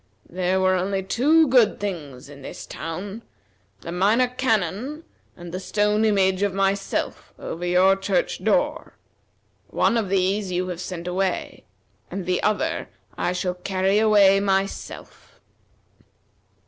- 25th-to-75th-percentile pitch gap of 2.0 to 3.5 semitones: Yes, narrow, 2.5 semitones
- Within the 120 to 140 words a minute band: Yes, slow, 135 wpm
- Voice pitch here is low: No, high, 195 Hz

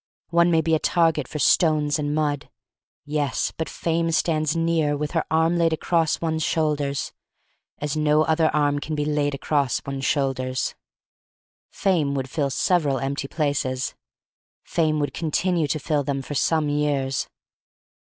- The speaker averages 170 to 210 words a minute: No, average, 160 wpm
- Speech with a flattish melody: Yes, narrow, 2.2 semitones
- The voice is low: No, medium, 150 Hz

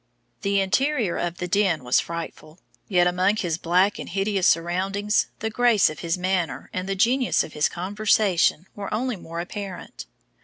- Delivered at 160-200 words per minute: Yes, average, 165 wpm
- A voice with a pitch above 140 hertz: Yes, medium, 185 Hz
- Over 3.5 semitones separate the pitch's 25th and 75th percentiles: No, average, 3.1 semitones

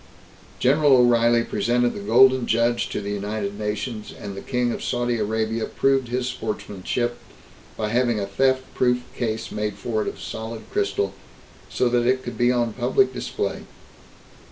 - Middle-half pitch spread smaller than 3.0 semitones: Yes, narrow, 2.5 semitones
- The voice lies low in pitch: Yes, low, 120 Hz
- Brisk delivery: No, average, 160 wpm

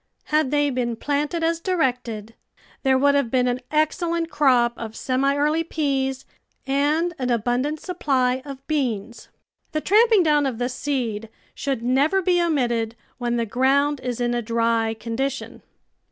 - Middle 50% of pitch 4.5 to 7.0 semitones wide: No, average, 3.8 semitones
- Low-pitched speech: No, very high, 270 Hz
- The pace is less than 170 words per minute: Yes, average, 155 wpm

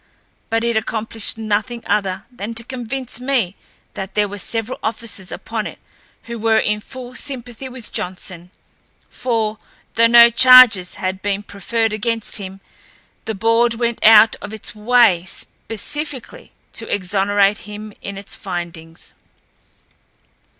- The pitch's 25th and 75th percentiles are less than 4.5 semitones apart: Yes, average, 2.8 semitones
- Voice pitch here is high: Yes, high, 220 Hz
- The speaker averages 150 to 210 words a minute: No, slow, 135 wpm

